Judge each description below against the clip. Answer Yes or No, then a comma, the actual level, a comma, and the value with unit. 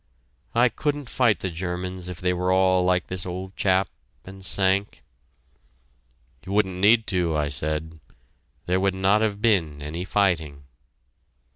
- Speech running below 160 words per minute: Yes, average, 145 wpm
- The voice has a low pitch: Yes, very low, 95 Hz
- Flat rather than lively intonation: Yes, narrow, 2.0 semitones